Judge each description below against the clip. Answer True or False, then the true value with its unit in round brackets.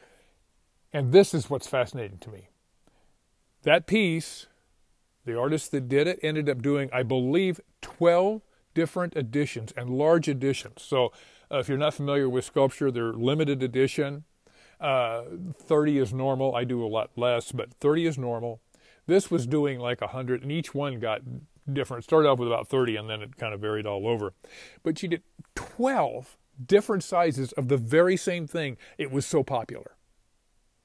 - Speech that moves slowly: False (170 wpm)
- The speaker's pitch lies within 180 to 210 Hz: False (140 Hz)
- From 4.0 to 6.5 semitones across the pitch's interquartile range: True (4.5 semitones)